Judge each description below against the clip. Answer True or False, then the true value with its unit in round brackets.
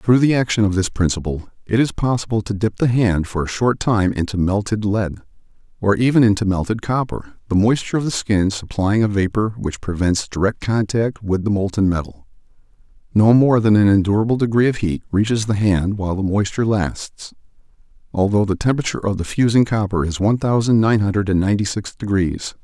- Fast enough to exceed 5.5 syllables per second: True (5.7 syllables/s)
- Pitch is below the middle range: True (105 Hz)